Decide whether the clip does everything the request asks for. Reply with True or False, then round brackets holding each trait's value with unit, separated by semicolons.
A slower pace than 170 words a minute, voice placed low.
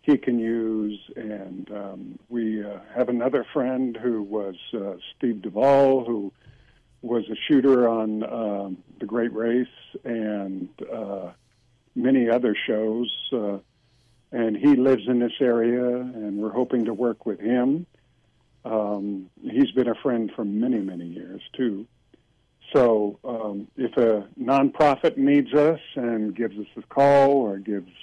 True (145 wpm; 120 Hz)